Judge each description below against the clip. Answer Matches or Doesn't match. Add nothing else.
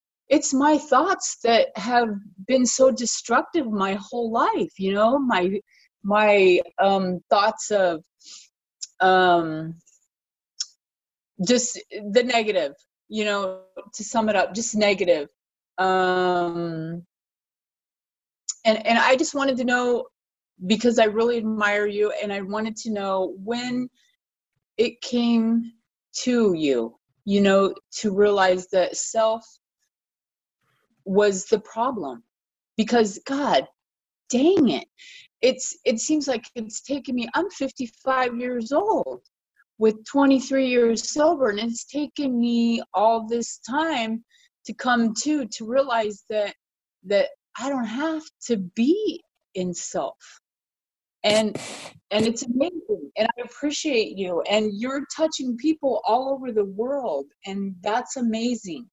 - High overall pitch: Matches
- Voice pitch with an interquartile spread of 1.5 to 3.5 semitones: Doesn't match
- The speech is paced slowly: Matches